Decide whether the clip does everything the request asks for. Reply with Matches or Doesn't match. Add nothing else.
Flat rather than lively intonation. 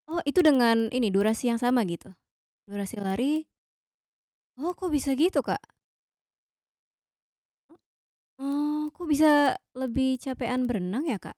Doesn't match